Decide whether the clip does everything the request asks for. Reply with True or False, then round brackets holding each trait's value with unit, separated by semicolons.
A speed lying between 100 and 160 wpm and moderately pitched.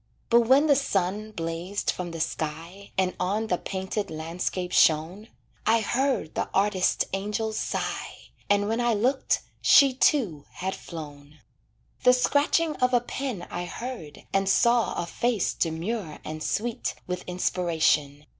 False (145 wpm; 195 Hz)